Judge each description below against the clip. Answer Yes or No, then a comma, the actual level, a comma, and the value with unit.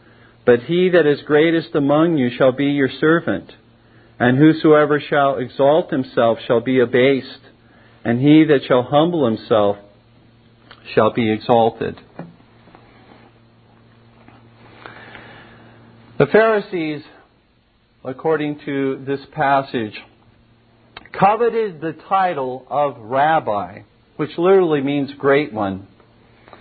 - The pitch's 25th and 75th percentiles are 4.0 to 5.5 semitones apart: Yes, average, 4.5 semitones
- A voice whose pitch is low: Yes, low, 125 Hz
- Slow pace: Yes, slow, 100 wpm